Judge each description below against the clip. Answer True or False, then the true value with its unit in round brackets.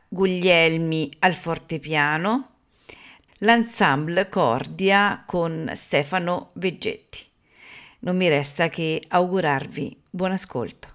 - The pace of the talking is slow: True (80 wpm)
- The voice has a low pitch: False (180 Hz)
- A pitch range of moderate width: True (3.2 semitones)